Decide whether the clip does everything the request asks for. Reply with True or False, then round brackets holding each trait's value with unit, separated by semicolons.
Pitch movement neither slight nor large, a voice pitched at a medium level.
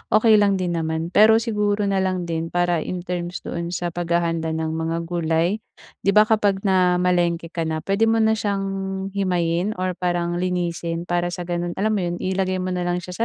False (2.3 semitones; 180 Hz)